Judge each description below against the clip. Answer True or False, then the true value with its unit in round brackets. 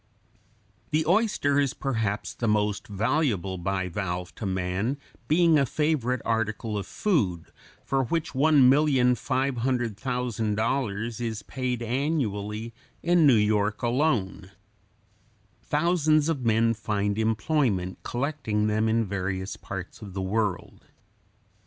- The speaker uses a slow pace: True (110 wpm)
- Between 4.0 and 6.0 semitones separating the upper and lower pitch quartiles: True (5.0 semitones)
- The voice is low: True (115 Hz)